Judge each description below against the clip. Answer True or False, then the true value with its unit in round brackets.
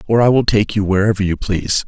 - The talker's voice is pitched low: True (100 Hz)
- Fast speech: True (255 wpm)